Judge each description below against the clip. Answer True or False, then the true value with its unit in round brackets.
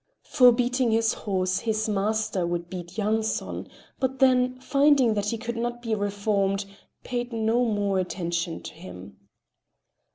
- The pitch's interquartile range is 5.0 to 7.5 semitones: False (3.7 semitones)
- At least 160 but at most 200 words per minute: False (140 wpm)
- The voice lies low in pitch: False (220 Hz)